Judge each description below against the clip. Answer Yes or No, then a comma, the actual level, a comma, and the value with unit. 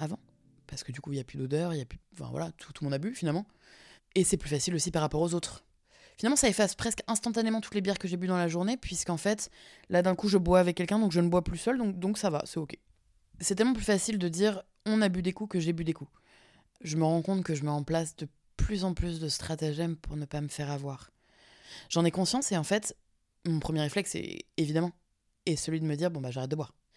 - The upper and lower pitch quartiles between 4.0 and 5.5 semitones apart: Yes, average, 4.6 semitones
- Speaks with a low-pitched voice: No, medium, 170 Hz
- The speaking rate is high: Yes, fast, 270 wpm